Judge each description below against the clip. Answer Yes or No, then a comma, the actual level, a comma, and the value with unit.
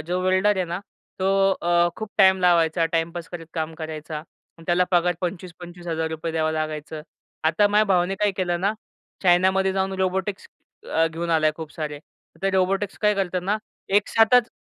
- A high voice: No, medium, 175 Hz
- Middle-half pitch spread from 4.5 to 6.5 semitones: No, average, 2.8 semitones